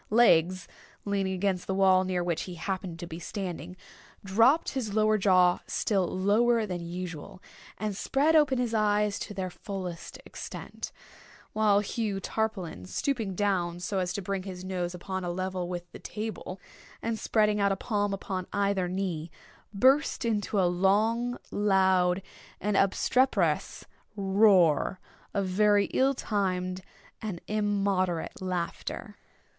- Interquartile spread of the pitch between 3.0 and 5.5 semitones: No, narrow, 2.6 semitones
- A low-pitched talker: No, high, 195 Hz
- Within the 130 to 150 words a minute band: Yes, average, 140 wpm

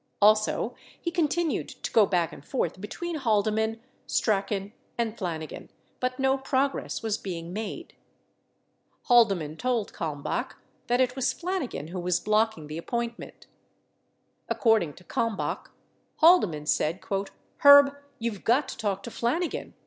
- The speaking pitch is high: Yes, high, 220 Hz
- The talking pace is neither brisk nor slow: No, slow, 130 wpm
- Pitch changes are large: Yes, wide, 5.8 semitones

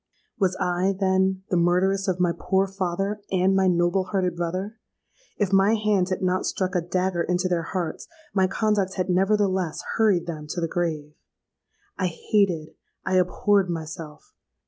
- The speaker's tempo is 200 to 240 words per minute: No, average, 155 wpm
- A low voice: No, medium, 185 Hz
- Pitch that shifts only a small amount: Yes, narrow, 1.8 semitones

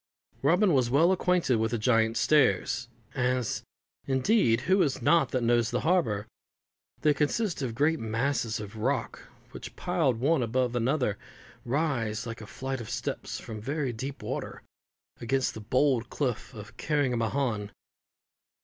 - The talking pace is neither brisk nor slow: Yes, average, 145 wpm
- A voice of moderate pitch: No, low, 125 Hz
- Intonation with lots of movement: No, average, 4.1 semitones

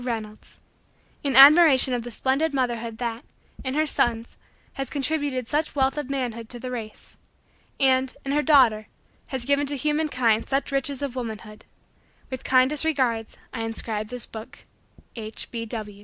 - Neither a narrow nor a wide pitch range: Yes, average, 3.5 semitones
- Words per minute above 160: No, average, 155 wpm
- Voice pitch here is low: No, very high, 255 Hz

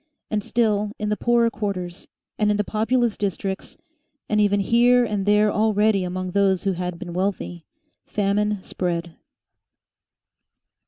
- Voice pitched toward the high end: Yes, high, 205 Hz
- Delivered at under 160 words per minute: Yes, average, 140 wpm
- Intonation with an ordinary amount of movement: No, narrow, 2.2 semitones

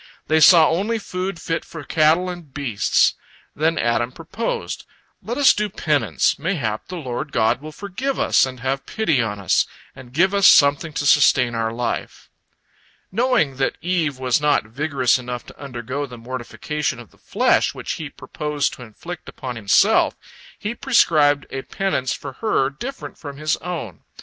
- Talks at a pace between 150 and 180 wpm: Yes, average, 165 wpm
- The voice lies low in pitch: No, medium, 145 Hz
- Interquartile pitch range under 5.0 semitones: No, wide, 5.5 semitones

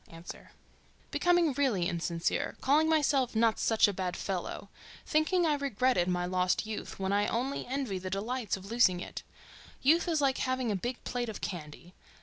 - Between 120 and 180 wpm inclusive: Yes, average, 160 wpm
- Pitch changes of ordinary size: No, wide, 6.8 semitones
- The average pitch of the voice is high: Yes, high, 225 Hz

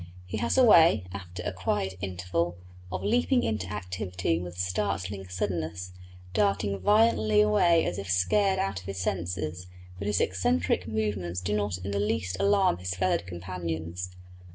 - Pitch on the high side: No, very low, 95 Hz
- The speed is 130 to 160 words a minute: Yes, average, 155 wpm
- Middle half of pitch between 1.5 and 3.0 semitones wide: Yes, narrow, 2.6 semitones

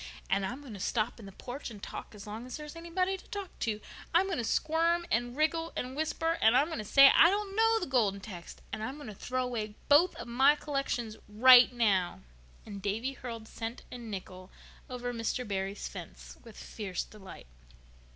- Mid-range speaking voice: No, high, 245 Hz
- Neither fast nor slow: No, fast, 210 wpm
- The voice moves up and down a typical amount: No, wide, 5.9 semitones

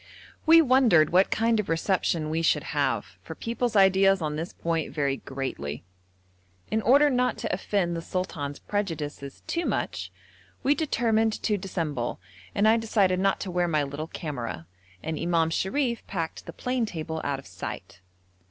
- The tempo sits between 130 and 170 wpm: Yes, average, 160 wpm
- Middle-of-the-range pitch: Yes, medium, 180 Hz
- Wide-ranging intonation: Yes, wide, 6.1 semitones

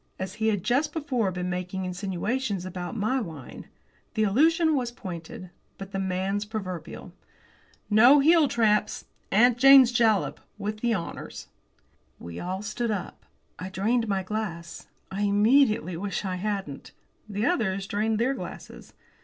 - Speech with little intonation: No, average, 4.3 semitones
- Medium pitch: No, high, 210 Hz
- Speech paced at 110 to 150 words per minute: Yes, average, 140 wpm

